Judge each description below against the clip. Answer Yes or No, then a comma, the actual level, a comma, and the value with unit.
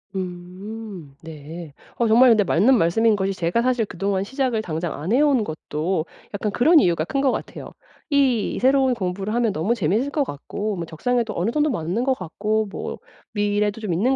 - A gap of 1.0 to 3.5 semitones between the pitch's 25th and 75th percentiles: No, wide, 5.5 semitones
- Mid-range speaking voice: No, high, 210 Hz